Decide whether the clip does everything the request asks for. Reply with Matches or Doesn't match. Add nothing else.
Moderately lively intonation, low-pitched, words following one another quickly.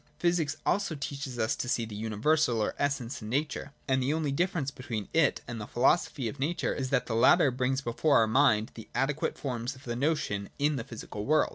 Matches